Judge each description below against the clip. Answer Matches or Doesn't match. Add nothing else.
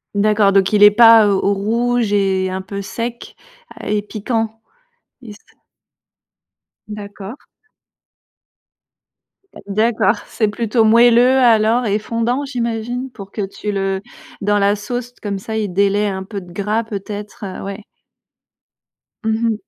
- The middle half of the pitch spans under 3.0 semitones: Matches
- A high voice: Matches